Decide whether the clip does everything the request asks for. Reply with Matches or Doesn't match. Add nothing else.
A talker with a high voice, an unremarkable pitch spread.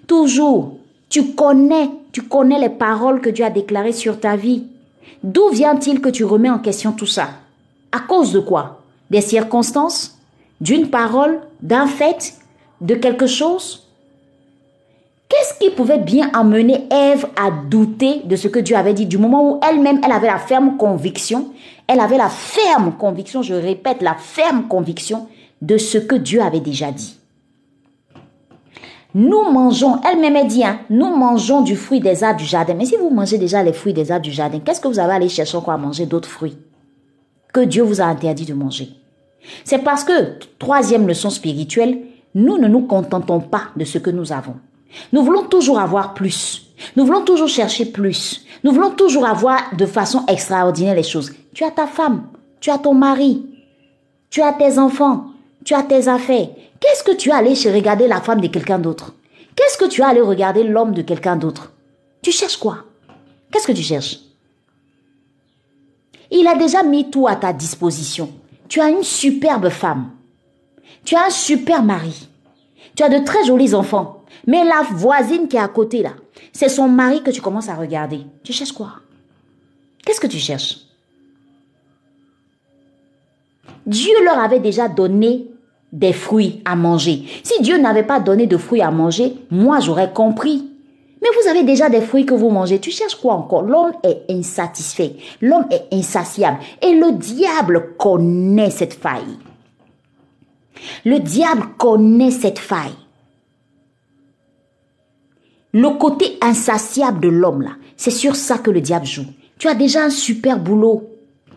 Doesn't match